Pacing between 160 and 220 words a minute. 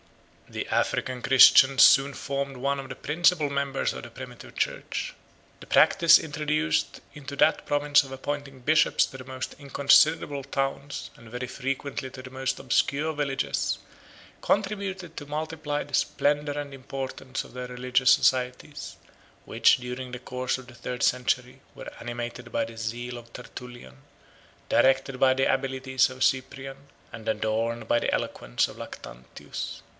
No: average, 150 wpm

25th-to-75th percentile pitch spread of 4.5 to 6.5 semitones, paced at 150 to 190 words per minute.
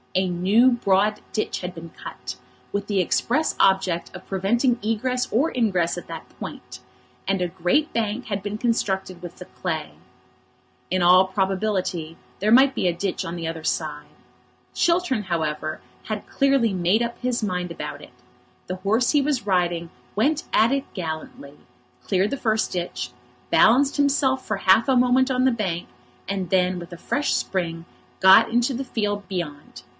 Yes: average, 5.2 semitones; average, 170 wpm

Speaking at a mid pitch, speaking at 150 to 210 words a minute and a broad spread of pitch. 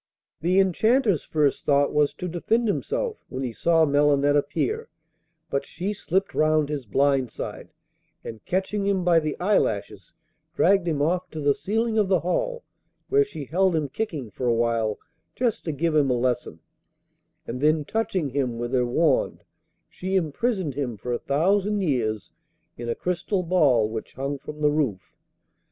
Yes: medium, 155 Hz; average, 170 wpm; wide, 6.1 semitones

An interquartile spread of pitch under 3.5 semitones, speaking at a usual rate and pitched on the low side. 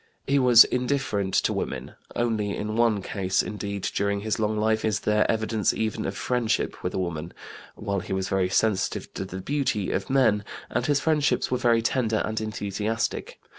Yes: average, 2.9 semitones; average, 180 wpm; low, 110 Hz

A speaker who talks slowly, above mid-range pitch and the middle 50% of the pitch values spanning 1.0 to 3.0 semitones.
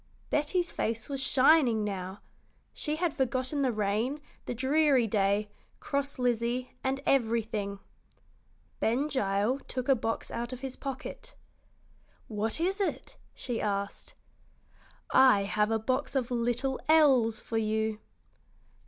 No: slow, 130 wpm; high, 245 Hz; average, 3.9 semitones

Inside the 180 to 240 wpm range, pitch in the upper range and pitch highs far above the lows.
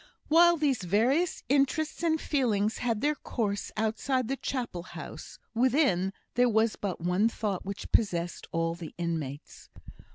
No: average, 140 wpm; high, 225 Hz; wide, 7.0 semitones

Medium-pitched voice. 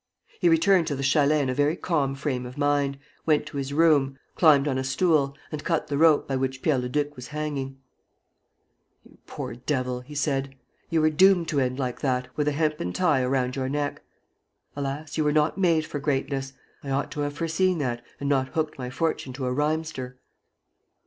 Yes: medium, 145 Hz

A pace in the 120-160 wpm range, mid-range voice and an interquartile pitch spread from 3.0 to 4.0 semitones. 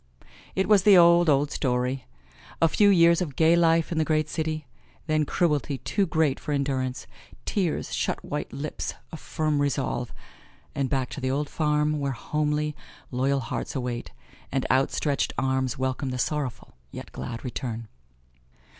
Yes: average, 155 wpm; medium, 145 Hz; average, 3.3 semitones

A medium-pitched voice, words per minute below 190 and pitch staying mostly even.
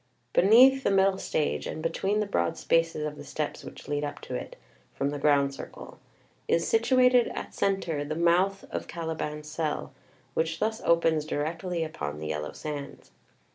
No: medium, 160 Hz; average, 170 wpm; average, 4.6 semitones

